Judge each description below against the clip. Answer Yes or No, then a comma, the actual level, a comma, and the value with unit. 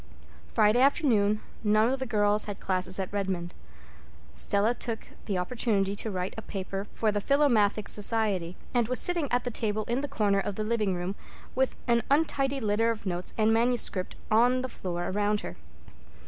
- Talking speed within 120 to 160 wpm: No, average, 175 wpm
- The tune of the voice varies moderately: Yes, average, 3.5 semitones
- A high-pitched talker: Yes, high, 215 Hz